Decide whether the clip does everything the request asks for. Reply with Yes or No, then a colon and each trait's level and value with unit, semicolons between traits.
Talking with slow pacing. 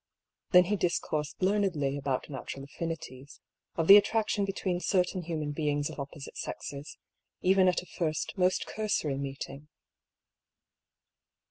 Yes: slow, 130 wpm